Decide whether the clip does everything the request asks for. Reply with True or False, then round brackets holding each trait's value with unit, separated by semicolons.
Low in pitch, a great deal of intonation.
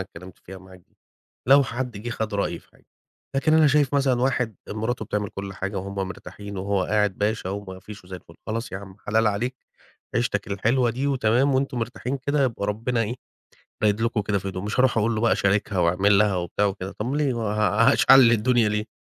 False (105 Hz; 3.7 semitones)